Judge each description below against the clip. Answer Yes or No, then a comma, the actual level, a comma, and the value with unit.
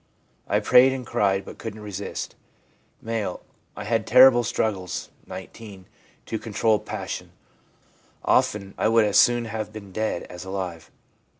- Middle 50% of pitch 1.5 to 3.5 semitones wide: Yes, average, 2.7 semitones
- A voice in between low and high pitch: No, low, 110 Hz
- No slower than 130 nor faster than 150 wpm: Yes, average, 140 wpm